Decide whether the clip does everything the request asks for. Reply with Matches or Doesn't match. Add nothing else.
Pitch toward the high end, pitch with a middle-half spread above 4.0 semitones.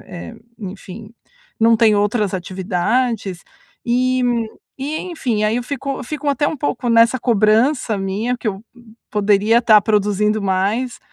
Doesn't match